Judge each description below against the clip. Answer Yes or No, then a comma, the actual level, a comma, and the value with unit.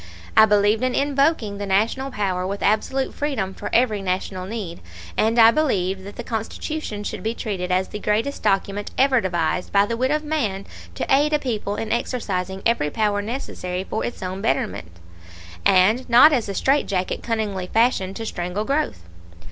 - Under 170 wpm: No, average, 175 wpm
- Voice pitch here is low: No, high, 210 Hz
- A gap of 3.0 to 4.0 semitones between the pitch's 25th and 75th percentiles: No, average, 4.6 semitones